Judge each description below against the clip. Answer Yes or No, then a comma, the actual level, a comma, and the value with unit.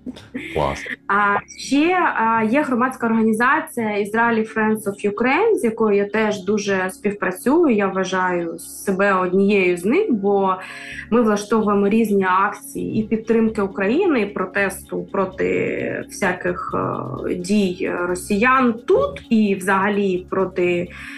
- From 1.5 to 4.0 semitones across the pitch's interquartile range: Yes, average, 3.2 semitones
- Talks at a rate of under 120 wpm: Yes, average, 110 wpm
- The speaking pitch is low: No, high, 205 Hz